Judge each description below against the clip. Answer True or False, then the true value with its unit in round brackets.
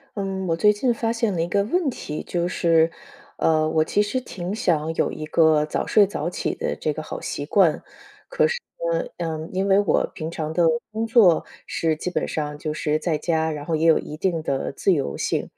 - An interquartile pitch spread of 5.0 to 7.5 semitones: False (4.2 semitones)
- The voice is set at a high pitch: False (165 Hz)